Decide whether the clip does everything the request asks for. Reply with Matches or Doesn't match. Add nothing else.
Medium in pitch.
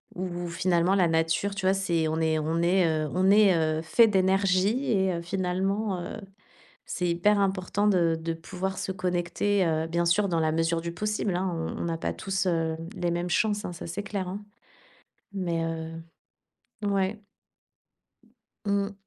Matches